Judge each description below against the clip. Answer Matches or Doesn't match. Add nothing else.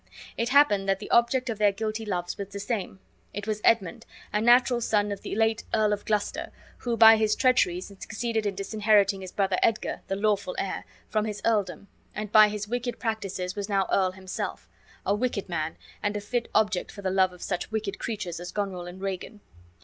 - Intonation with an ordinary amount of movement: Doesn't match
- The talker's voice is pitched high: Matches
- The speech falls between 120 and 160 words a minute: Doesn't match